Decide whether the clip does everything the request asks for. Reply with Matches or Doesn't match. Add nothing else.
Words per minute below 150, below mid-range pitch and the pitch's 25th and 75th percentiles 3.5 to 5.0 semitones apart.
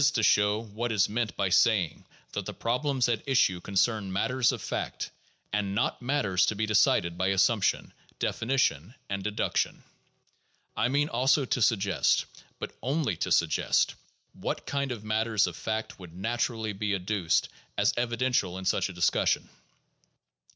Doesn't match